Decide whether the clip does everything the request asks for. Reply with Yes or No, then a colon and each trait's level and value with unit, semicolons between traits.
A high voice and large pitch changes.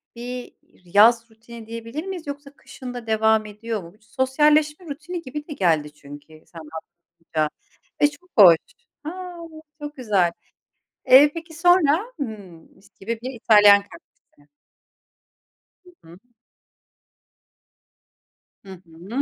Yes: high, 230 Hz; wide, 7.2 semitones